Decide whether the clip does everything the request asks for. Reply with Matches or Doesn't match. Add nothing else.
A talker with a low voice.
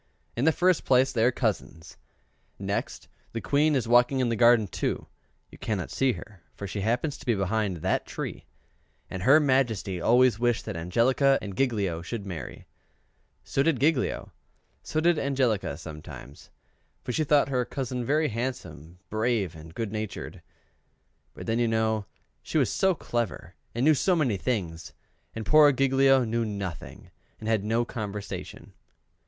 Matches